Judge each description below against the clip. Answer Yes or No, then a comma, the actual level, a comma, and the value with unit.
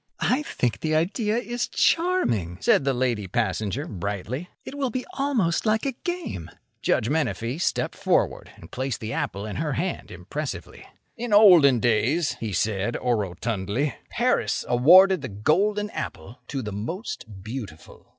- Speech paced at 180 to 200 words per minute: No, average, 150 wpm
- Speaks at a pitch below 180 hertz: Yes, low, 135 Hz